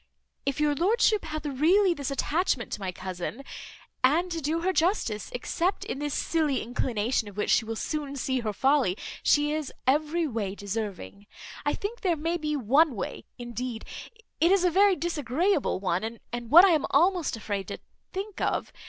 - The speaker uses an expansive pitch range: Yes, wide, 6.7 semitones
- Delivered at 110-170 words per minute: No, average, 180 wpm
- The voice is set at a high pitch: Yes, very high, 290 Hz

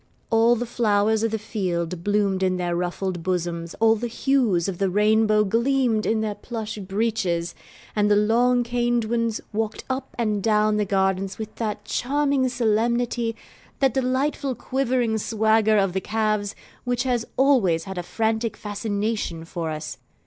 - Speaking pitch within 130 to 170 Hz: No, high, 220 Hz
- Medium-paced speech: Yes, average, 155 wpm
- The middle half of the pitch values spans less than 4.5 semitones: Yes, average, 3.4 semitones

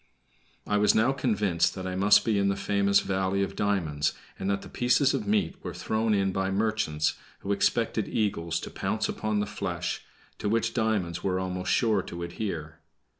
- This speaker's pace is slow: No, average, 185 wpm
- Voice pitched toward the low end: Yes, low, 100 Hz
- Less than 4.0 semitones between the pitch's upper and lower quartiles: Yes, average, 2.9 semitones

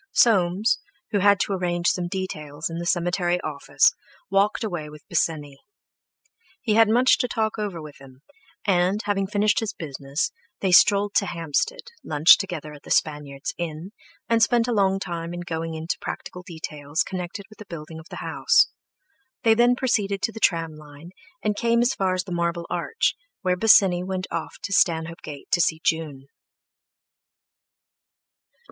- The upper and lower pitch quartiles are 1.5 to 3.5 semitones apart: No, average, 4.0 semitones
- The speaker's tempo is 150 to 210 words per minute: Yes, average, 165 wpm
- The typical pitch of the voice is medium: Yes, medium, 175 Hz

